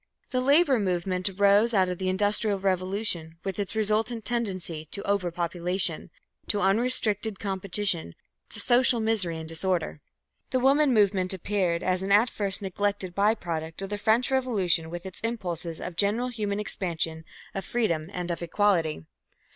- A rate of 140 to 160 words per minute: Yes, average, 155 wpm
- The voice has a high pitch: Yes, high, 195 Hz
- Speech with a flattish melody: No, average, 3.5 semitones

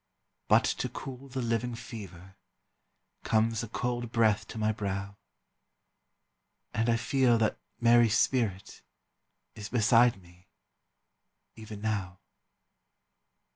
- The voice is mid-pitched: No, low, 110 Hz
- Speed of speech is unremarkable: No, slow, 105 wpm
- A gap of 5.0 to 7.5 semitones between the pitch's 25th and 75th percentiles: No, average, 2.8 semitones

